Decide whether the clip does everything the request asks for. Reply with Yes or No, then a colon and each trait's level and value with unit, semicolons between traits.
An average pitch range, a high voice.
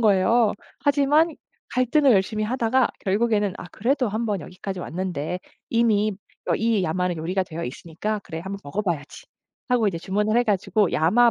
Yes: average, 4.3 semitones; high, 210 Hz